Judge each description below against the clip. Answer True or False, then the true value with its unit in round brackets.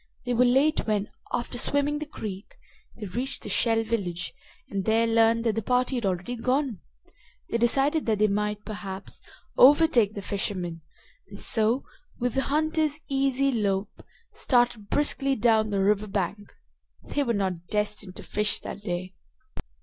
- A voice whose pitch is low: False (225 Hz)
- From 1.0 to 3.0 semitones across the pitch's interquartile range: False (4.3 semitones)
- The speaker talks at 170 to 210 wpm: False (155 wpm)